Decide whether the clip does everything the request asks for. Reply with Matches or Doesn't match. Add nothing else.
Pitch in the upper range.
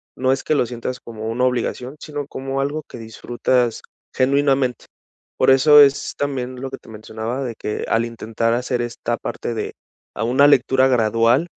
Doesn't match